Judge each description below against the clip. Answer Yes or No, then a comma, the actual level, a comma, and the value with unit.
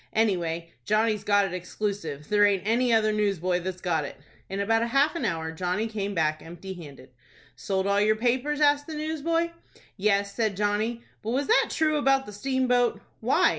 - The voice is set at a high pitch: Yes, high, 210 Hz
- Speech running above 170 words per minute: Yes, average, 180 wpm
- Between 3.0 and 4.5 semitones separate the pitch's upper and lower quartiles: No, average, 5.2 semitones